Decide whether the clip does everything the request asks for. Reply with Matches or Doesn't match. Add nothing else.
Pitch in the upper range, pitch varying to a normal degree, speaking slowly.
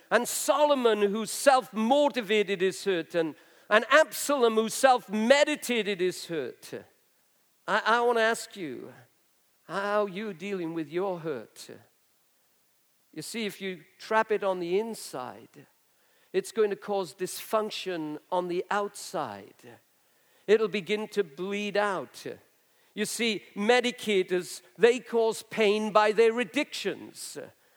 Matches